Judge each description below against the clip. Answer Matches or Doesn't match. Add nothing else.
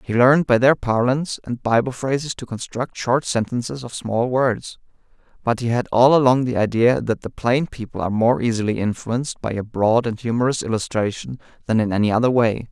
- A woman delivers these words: Doesn't match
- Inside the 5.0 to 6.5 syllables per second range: Matches